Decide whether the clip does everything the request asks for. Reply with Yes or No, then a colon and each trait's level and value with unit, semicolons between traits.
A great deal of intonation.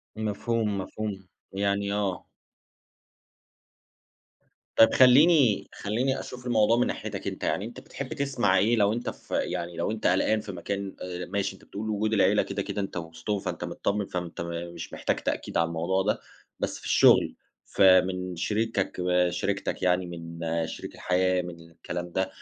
No: average, 3.2 semitones